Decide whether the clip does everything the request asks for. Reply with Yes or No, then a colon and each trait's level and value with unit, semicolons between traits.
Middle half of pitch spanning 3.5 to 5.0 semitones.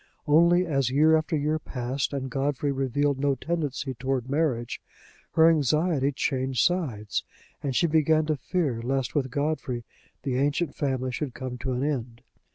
No: average, 3.1 semitones